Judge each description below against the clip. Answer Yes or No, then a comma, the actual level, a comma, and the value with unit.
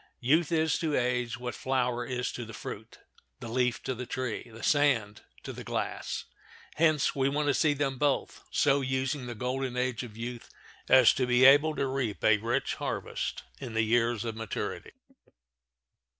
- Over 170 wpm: Yes, average, 180 wpm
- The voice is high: No, low, 125 Hz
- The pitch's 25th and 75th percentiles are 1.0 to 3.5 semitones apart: Yes, narrow, 2.4 semitones